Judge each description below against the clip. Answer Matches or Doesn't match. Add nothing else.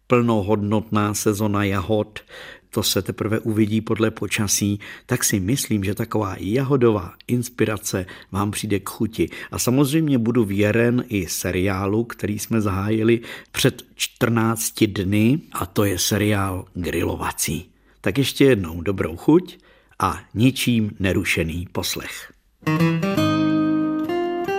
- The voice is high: Doesn't match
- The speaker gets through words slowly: Matches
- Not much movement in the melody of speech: Doesn't match